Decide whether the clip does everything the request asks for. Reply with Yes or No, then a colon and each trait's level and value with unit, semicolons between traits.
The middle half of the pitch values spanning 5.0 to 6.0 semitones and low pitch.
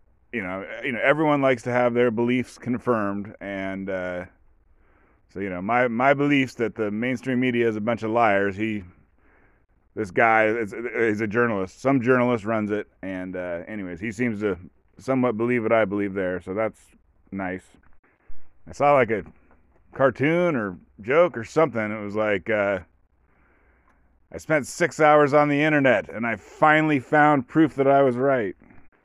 Yes: average, 5.3 semitones; low, 110 Hz